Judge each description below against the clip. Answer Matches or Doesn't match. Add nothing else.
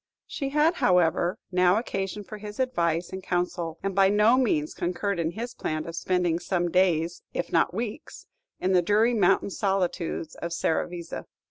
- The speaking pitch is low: Doesn't match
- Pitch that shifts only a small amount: Doesn't match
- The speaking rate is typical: Matches